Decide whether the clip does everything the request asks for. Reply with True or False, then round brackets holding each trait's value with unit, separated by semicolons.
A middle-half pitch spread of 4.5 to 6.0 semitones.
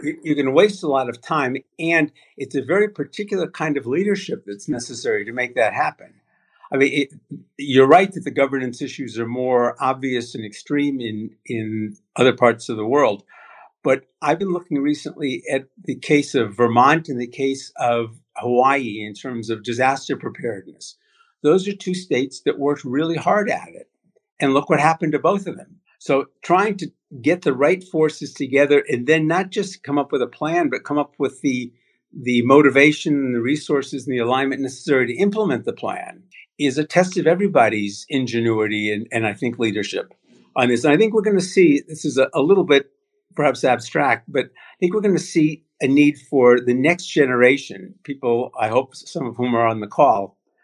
True (4.9 semitones)